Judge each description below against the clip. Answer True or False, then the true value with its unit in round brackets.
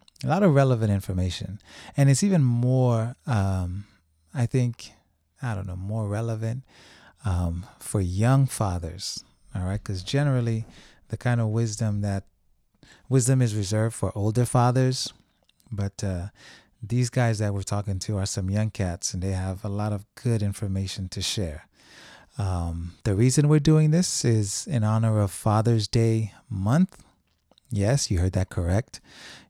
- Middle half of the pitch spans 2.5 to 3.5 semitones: False (4.0 semitones)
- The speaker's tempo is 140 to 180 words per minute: True (155 wpm)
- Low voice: True (105 Hz)